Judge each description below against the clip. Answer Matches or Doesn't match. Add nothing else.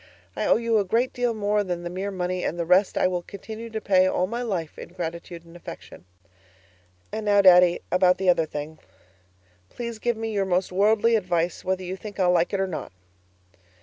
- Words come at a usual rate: Doesn't match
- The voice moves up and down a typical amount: Matches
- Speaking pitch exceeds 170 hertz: Matches